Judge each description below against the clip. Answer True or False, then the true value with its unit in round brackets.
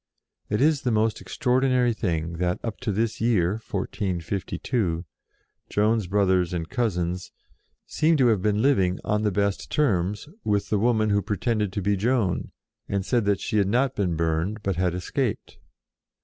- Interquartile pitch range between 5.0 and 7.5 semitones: False (4.0 semitones)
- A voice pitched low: True (105 Hz)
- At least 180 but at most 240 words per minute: False (165 wpm)